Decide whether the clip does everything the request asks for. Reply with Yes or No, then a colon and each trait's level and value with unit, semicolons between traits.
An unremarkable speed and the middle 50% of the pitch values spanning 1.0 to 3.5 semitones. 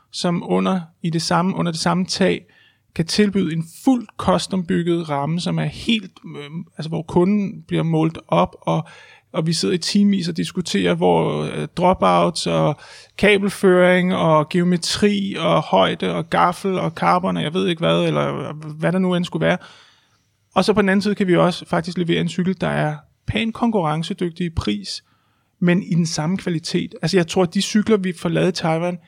Yes: average, 190 wpm; average, 3.1 semitones